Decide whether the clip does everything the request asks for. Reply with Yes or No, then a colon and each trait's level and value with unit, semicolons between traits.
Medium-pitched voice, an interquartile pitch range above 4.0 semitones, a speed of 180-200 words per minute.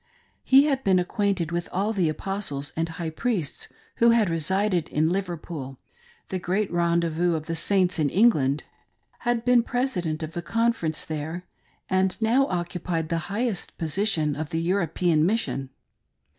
No: medium, 175 Hz; average, 4.4 semitones; average, 155 wpm